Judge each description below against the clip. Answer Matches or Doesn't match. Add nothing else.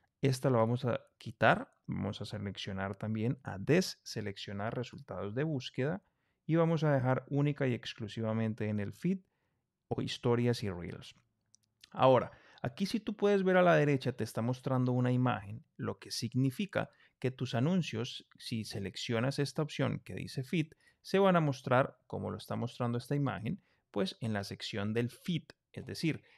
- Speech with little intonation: Doesn't match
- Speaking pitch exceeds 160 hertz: Doesn't match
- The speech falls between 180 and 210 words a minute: Doesn't match